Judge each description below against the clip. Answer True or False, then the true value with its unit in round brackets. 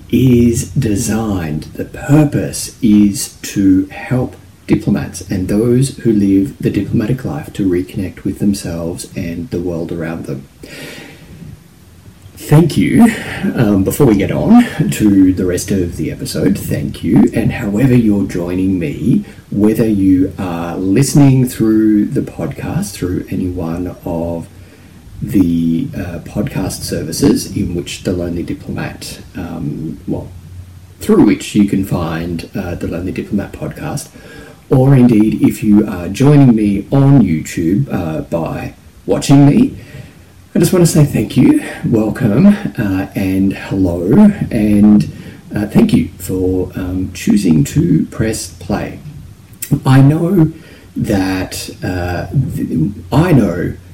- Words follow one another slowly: True (130 wpm)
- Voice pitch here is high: False (100 Hz)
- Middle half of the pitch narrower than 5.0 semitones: False (5.3 semitones)